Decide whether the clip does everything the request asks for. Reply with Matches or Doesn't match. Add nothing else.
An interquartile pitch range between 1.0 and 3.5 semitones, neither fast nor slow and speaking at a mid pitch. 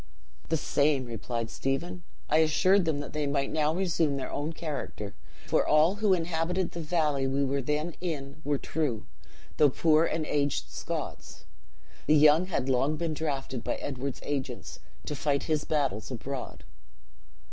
Matches